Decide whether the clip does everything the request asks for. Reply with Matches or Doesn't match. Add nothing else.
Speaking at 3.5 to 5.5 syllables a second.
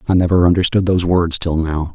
Doesn't match